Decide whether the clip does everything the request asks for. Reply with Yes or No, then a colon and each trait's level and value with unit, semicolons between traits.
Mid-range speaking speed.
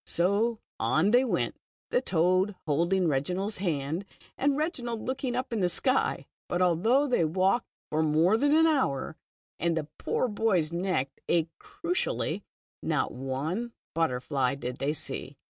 Yes: average, 145 wpm